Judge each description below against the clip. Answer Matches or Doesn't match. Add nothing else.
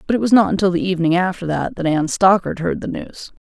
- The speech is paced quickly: Matches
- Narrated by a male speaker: Doesn't match